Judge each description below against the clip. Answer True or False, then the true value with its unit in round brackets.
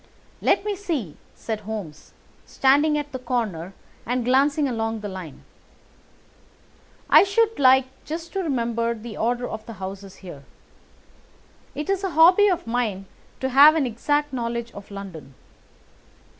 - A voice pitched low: False (245 Hz)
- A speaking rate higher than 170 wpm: False (145 wpm)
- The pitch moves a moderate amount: False (6.0 semitones)